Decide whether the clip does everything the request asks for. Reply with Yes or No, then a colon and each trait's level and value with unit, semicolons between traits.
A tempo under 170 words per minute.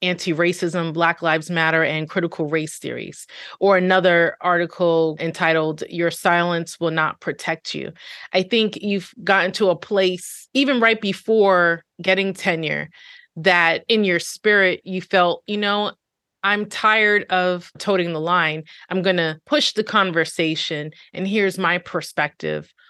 Yes: average, 145 wpm